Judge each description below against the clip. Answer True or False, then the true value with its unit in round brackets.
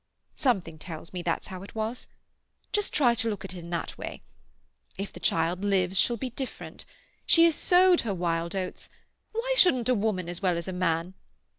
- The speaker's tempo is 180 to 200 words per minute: True (190 wpm)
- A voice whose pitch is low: False (195 Hz)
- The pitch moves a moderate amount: False (5.7 semitones)